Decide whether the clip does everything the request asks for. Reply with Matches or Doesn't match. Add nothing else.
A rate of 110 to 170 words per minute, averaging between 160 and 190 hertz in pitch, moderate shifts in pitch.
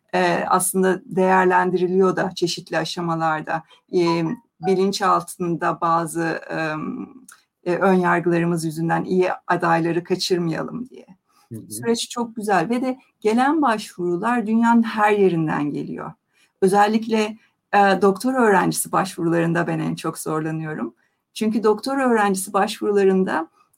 Doesn't match